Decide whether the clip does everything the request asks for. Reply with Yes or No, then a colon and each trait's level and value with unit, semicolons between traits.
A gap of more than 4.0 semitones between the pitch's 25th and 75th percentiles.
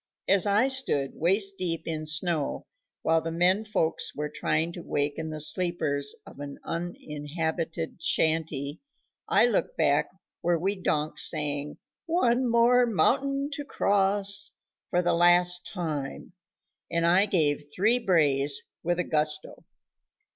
Yes: average, 4.4 semitones